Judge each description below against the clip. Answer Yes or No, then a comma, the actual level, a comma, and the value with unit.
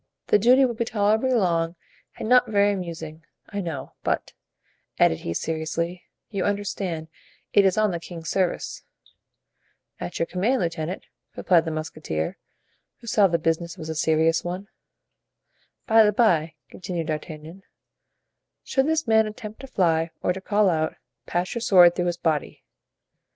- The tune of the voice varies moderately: Yes, average, 4.4 semitones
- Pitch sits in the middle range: Yes, medium, 180 Hz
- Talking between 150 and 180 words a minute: Yes, average, 155 wpm